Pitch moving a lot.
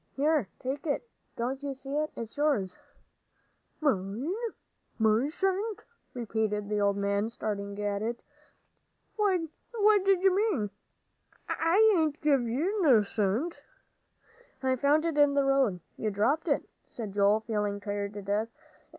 Yes: wide, 7.1 semitones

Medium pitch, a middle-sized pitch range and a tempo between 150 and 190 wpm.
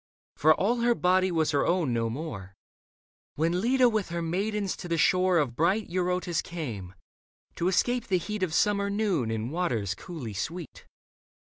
Yes: medium, 175 Hz; average, 5.0 semitones; average, 170 wpm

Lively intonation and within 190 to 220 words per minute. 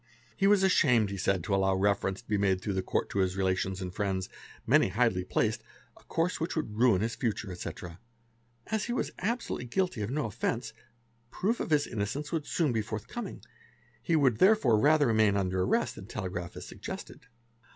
Yes: wide, 7.7 semitones; average, 195 wpm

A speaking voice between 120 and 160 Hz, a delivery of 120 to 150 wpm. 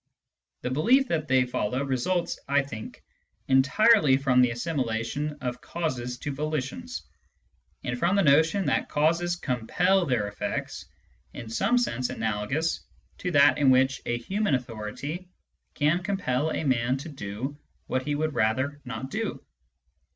Yes: medium, 140 Hz; average, 145 wpm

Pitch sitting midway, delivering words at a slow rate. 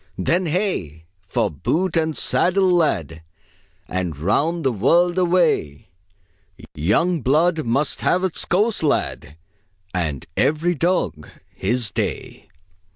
Yes: medium, 155 Hz; slow, 110 wpm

